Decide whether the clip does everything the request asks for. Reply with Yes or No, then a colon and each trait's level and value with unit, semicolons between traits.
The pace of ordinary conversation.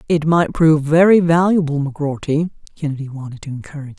Yes: average, 165 wpm